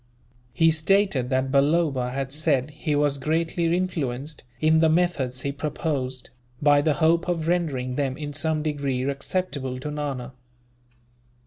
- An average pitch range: Yes, average, 3.3 semitones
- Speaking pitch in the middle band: Yes, medium, 145 Hz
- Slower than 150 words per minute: Yes, average, 140 wpm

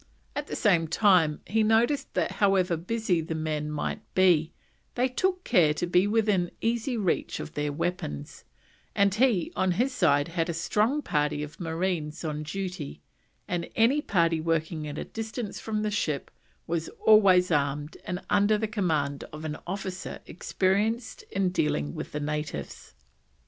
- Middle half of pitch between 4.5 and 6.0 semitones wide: Yes, wide, 5.6 semitones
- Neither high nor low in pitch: Yes, medium, 180 Hz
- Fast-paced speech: No, average, 160 wpm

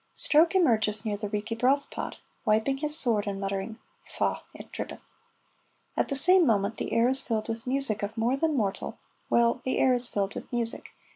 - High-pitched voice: Yes, high, 230 Hz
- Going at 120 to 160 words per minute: No, average, 195 wpm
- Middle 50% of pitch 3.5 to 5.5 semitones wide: Yes, average, 4.1 semitones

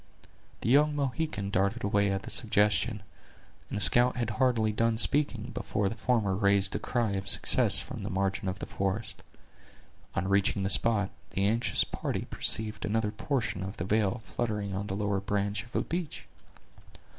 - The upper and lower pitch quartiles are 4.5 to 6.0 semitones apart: No, average, 2.8 semitones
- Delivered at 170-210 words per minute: Yes, average, 175 wpm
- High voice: No, low, 105 Hz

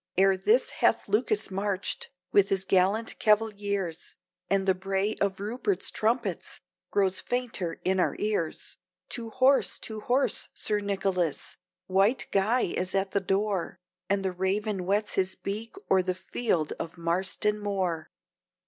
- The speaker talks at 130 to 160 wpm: Yes, average, 140 wpm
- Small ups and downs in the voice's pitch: Yes, narrow, 2.2 semitones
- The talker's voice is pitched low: No, high, 195 Hz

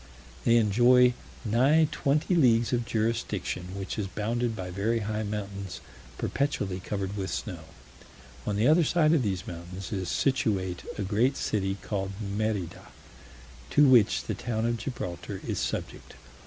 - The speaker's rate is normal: Yes, average, 145 wpm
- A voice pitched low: Yes, low, 105 Hz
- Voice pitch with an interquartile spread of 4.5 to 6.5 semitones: No, average, 3.8 semitones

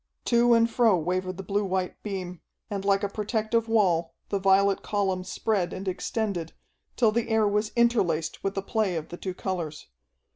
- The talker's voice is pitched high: Yes, high, 195 Hz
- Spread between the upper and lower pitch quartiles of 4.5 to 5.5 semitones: No, average, 3.0 semitones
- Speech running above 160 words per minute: Yes, average, 180 wpm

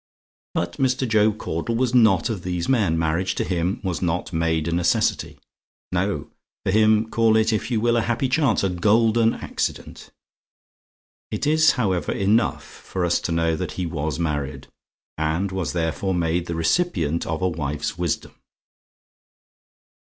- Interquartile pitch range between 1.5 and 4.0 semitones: No, average, 5.1 semitones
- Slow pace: No, average, 160 wpm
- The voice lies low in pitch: Yes, very low, 95 Hz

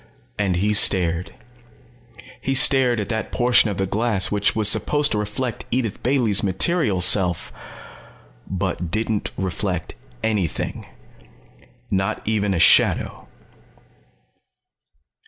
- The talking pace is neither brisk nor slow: No, slow, 110 wpm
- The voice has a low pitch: Yes, low, 105 Hz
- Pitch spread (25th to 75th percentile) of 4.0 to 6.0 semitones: No, average, 3.5 semitones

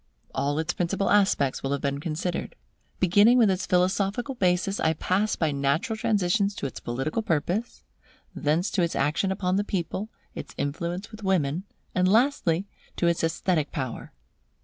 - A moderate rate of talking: Yes, average, 160 wpm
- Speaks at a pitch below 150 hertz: No, medium, 180 Hz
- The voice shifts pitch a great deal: No, average, 4.4 semitones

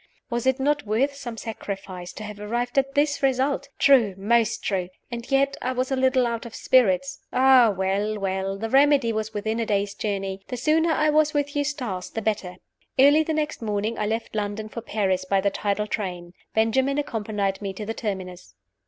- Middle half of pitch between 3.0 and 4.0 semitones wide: No, average, 4.9 semitones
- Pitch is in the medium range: No, high, 225 Hz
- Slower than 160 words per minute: No, average, 195 wpm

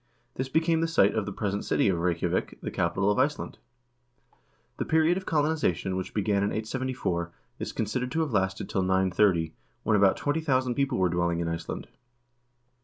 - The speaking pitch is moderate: No, low, 105 Hz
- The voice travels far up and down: Yes, wide, 6.7 semitones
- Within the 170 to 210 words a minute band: Yes, average, 175 wpm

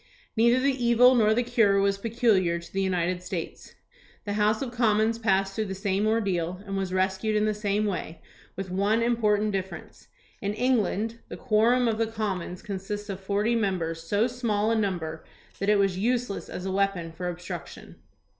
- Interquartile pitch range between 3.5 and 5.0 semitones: No, average, 3.0 semitones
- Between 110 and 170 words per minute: No, average, 185 wpm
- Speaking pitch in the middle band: No, high, 205 Hz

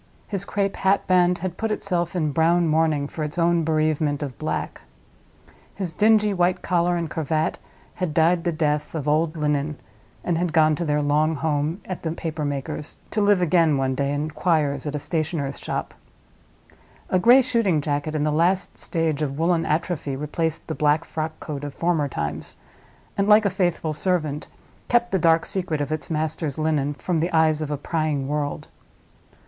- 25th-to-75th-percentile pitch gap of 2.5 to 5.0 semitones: Yes, average, 2.9 semitones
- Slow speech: No, average, 180 wpm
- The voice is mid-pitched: Yes, medium, 160 Hz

